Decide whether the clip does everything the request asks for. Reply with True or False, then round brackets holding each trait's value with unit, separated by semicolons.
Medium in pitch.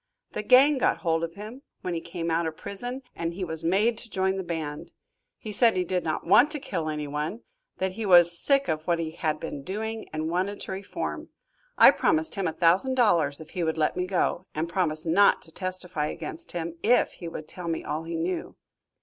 True (175 Hz)